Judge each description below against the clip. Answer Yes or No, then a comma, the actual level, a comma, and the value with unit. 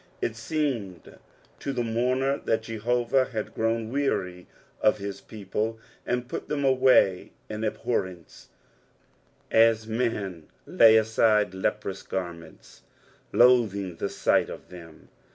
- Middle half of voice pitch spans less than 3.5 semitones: No, average, 4.1 semitones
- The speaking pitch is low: Yes, low, 110 Hz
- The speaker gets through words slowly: Yes, slow, 115 wpm